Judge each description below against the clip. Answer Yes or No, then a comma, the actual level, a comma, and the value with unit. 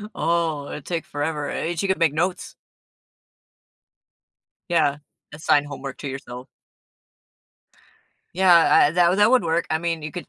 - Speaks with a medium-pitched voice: Yes, medium, 160 Hz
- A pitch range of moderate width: Yes, average, 3.0 semitones